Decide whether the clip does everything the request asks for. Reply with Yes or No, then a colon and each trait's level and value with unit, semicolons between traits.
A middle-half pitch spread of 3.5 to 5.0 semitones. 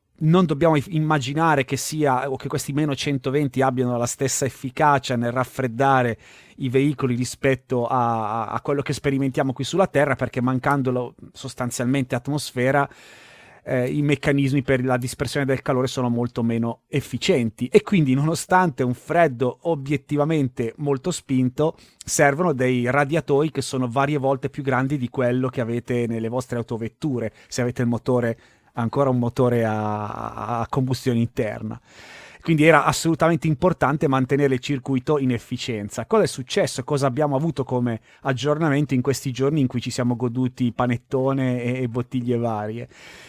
No: average, 2.7 semitones